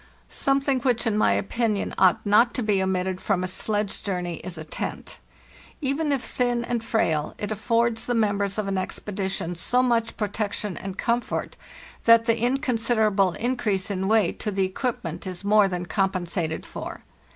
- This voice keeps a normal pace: Yes, average, 165 wpm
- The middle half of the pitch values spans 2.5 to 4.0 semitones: Yes, average, 3.7 semitones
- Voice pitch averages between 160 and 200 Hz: No, high, 210 Hz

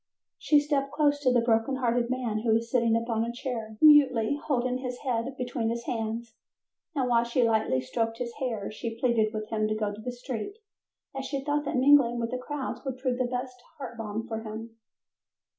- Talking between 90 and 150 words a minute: No, fast, 205 wpm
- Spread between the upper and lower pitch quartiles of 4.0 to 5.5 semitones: No, narrow, 2.4 semitones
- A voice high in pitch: Yes, high, 240 Hz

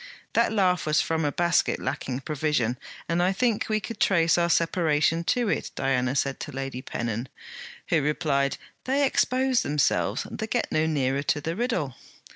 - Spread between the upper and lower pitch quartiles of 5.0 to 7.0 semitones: Yes, wide, 5.4 semitones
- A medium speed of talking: Yes, average, 170 wpm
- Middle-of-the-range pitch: Yes, medium, 160 Hz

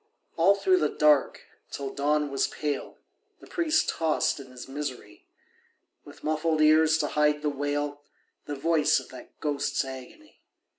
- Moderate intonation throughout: No, narrow, 1.9 semitones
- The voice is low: No, medium, 150 Hz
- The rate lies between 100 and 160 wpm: Yes, average, 150 wpm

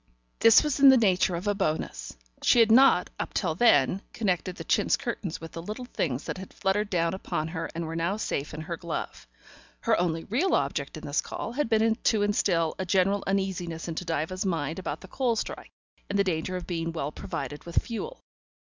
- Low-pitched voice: No, medium, 185 Hz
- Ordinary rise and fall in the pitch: Yes, average, 4.3 semitones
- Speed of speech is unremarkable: No, fast, 210 wpm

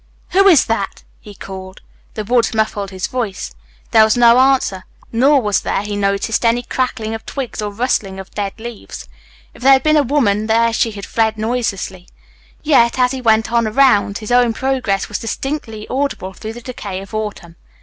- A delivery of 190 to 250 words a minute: Yes, average, 195 wpm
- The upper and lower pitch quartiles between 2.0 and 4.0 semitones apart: Yes, average, 3.5 semitones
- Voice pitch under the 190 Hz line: No, high, 225 Hz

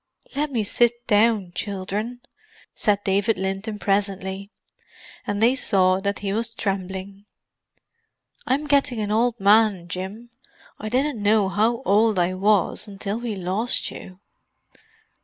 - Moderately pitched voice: No, high, 205 Hz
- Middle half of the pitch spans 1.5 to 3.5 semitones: Yes, average, 2.9 semitones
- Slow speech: Yes, slow, 130 wpm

